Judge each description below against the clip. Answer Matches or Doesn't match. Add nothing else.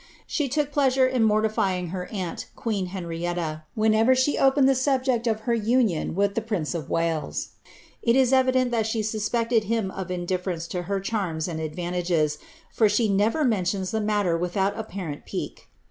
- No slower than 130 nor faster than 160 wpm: Doesn't match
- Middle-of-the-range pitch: Doesn't match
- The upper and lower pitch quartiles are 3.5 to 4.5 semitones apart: Doesn't match